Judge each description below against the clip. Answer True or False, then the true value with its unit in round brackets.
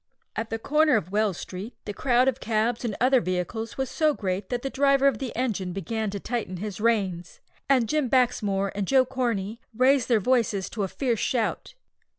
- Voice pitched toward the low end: False (230 Hz)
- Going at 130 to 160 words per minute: False (195 wpm)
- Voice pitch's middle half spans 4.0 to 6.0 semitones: True (4.4 semitones)